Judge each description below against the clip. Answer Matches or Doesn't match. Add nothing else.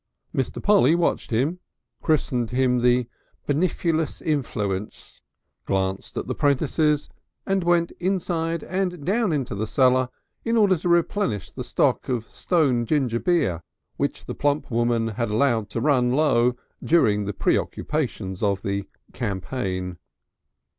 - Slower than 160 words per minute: Matches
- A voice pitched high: Doesn't match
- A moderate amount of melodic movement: Doesn't match